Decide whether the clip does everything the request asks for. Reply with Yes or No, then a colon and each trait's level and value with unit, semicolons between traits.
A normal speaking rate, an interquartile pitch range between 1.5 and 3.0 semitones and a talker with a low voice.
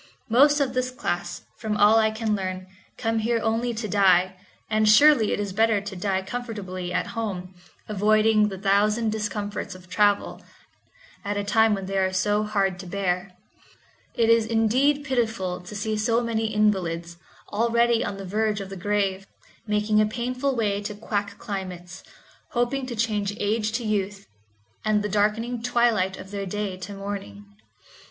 No: average, 165 wpm; narrow, 2.5 semitones; high, 210 Hz